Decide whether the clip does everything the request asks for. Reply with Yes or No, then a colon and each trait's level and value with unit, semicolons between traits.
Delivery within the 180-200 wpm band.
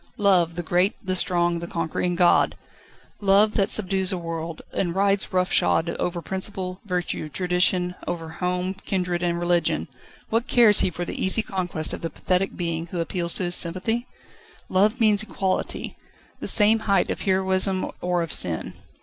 No: average, 165 wpm